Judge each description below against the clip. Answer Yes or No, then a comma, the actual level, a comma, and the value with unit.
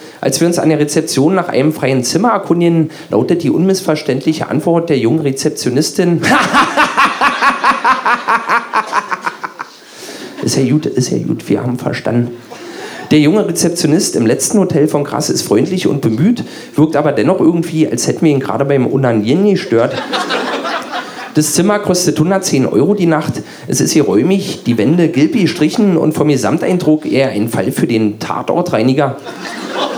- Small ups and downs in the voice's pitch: No, average, 3.8 semitones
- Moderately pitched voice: Yes, medium, 155 Hz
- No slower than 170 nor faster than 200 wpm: No, average, 150 wpm